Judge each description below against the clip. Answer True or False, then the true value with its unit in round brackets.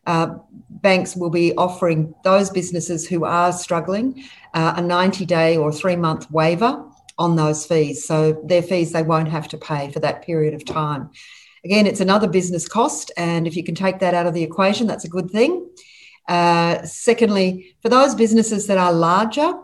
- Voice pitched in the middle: True (175 Hz)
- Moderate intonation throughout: True (3.3 semitones)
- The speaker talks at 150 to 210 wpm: True (185 wpm)